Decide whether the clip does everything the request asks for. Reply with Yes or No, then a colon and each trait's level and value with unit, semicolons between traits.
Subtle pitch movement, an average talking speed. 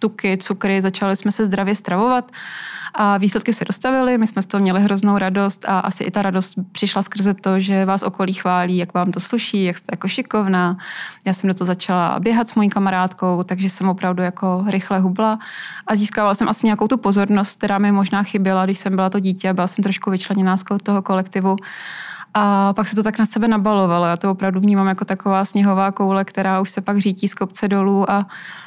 No: narrow, 1.4 semitones; fast, 210 wpm